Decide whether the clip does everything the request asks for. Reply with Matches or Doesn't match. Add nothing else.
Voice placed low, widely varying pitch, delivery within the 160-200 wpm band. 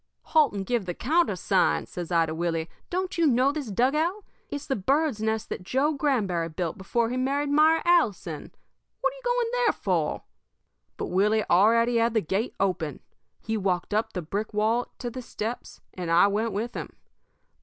Doesn't match